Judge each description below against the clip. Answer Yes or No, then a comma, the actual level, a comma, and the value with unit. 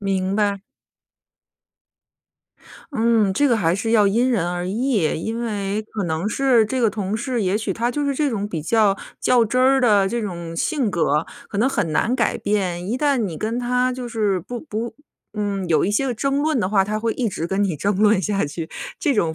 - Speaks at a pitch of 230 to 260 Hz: No, high, 215 Hz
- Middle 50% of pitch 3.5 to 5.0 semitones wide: Yes, average, 4.0 semitones